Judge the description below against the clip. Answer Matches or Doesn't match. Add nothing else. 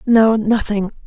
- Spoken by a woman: Matches